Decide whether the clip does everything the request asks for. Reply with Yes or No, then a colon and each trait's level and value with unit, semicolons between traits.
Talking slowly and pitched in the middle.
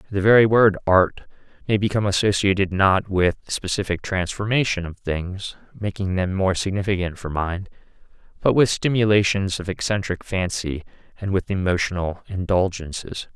No: slow, 130 wpm; very low, 95 Hz